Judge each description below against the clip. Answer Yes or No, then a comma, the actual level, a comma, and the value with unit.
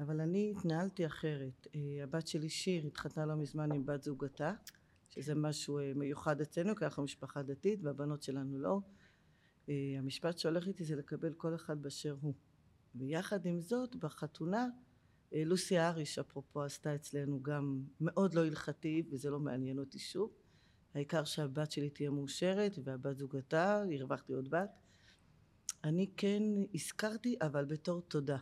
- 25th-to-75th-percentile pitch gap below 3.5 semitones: Yes, average, 3.1 semitones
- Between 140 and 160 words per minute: Yes, fast, 150 wpm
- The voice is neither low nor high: Yes, medium, 150 Hz